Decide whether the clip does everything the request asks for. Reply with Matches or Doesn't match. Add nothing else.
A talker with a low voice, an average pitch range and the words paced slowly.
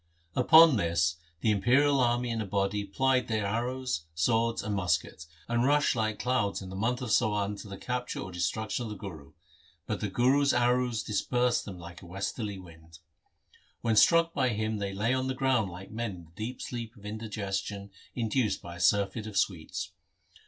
Doesn't match